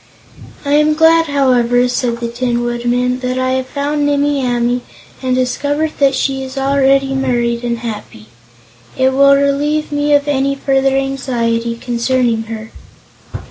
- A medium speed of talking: Yes, average, 145 wpm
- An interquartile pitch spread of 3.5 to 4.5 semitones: No, narrow, 2.6 semitones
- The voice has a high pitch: Yes, very high, 260 Hz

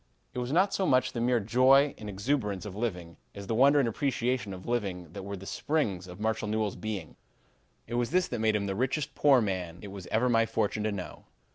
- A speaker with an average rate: No, fast, 230 wpm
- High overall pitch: No, low, 110 Hz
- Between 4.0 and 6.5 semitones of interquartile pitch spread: Yes, average, 4.3 semitones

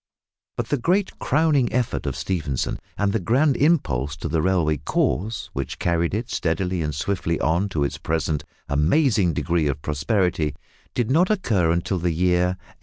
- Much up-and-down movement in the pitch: Yes, wide, 6.6 semitones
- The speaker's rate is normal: Yes, average, 170 wpm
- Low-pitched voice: Yes, very low, 90 Hz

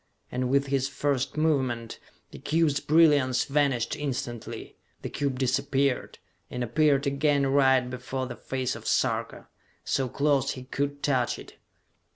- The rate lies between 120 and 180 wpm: Yes, average, 140 wpm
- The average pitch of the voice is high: No, low, 135 Hz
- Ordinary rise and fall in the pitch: No, narrow, 1.9 semitones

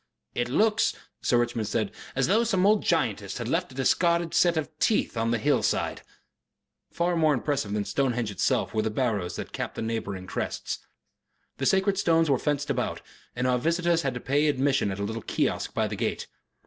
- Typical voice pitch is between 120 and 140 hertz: Yes, low, 135 Hz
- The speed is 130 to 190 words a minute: No, average, 200 wpm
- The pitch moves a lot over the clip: Yes, wide, 6.8 semitones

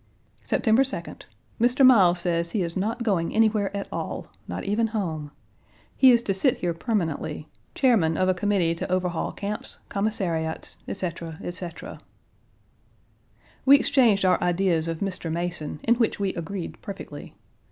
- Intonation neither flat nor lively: Yes, average, 4.5 semitones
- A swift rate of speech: No, average, 145 wpm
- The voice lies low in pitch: No, high, 190 Hz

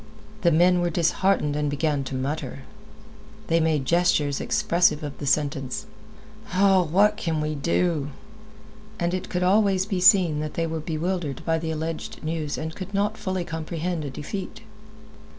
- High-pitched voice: No, medium, 165 Hz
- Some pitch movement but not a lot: Yes, average, 3.3 semitones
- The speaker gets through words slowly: No, average, 165 wpm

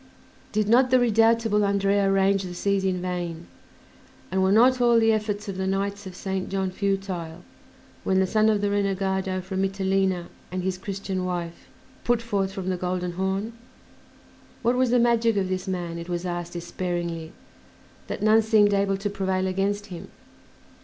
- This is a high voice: Yes, high, 195 Hz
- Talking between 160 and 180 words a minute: Yes, average, 175 wpm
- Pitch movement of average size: No, narrow, 2.0 semitones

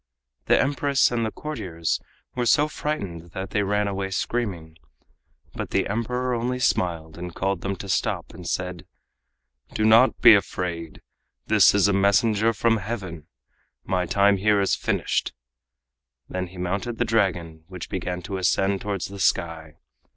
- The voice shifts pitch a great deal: No, average, 3.9 semitones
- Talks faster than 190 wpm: No, average, 160 wpm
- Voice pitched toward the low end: Yes, low, 100 Hz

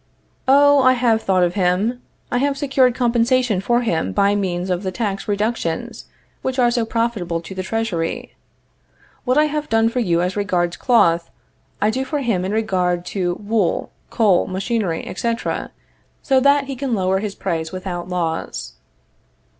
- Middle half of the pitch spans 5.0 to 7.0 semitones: Yes, average, 5.3 semitones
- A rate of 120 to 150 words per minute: No, average, 165 wpm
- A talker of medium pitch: No, high, 210 Hz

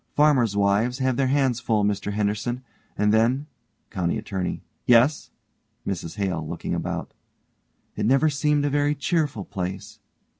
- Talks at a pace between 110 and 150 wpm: Yes, average, 140 wpm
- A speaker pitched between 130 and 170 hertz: No, low, 115 Hz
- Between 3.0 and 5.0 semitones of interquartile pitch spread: No, wide, 5.5 semitones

